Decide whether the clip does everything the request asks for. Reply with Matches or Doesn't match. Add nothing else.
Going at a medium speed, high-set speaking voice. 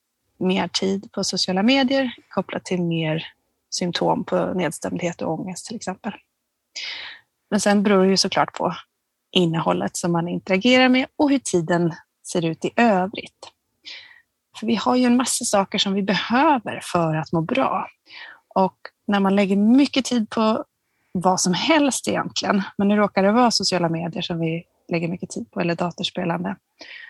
Matches